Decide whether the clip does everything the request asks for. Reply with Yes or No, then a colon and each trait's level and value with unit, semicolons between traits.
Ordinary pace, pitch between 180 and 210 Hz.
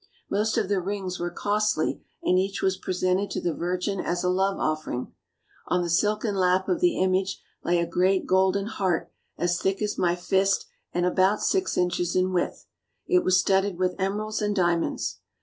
Yes: average, 185 wpm; medium, 185 Hz